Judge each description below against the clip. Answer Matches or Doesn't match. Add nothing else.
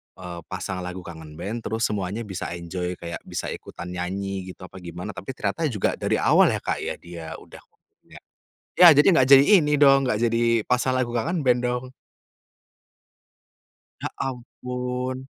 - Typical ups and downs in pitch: Doesn't match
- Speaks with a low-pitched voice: Matches